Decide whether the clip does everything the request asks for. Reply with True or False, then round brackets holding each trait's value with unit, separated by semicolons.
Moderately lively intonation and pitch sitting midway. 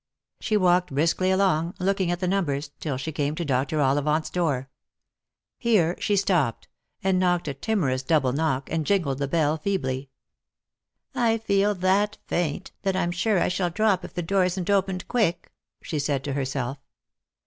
True (5.0 semitones; 170 Hz)